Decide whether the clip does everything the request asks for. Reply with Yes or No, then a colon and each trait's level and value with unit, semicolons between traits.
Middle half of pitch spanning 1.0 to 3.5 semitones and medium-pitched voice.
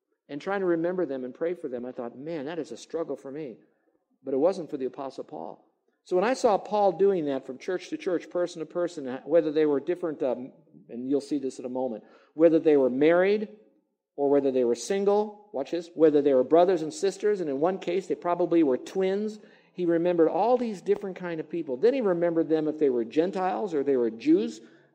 No: average, 4.9 semitones; medium, 170 Hz